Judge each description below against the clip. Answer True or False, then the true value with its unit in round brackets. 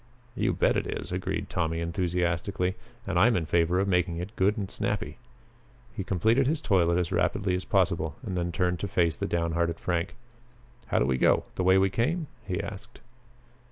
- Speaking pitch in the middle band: False (90 Hz)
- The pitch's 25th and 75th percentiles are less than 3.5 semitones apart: True (2.6 semitones)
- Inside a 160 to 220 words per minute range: True (190 wpm)